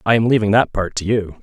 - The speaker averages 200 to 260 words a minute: No, fast, 295 wpm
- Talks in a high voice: No, low, 105 Hz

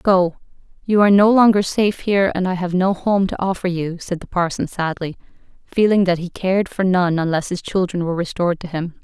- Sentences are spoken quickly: Yes, fast, 210 wpm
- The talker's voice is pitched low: No, medium, 185 Hz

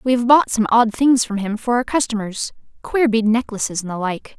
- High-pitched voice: Yes, high, 230 Hz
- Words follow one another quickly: Yes, fast, 235 wpm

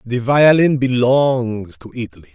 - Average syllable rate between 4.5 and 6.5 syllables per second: No, 4.1 syllables/s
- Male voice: Yes, male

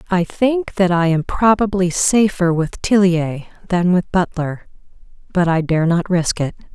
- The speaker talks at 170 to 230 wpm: No, average, 160 wpm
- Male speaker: No, female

